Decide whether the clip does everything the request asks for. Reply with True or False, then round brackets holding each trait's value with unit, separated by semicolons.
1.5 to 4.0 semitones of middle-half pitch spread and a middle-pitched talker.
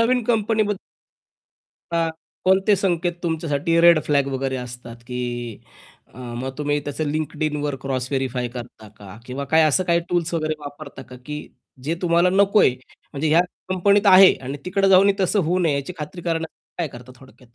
False (5.2 semitones; 155 Hz)